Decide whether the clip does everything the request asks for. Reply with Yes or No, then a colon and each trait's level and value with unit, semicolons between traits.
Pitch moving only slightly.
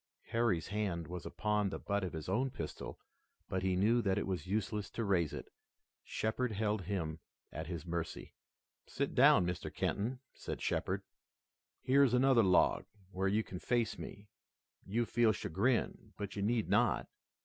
No: average, 3.8 semitones